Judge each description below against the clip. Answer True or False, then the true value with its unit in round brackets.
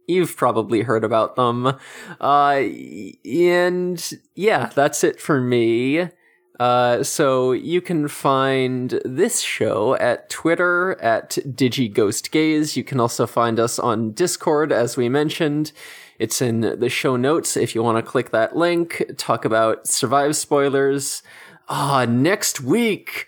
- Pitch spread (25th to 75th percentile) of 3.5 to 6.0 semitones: True (4.7 semitones)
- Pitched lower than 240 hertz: True (135 Hz)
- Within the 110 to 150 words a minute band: True (135 wpm)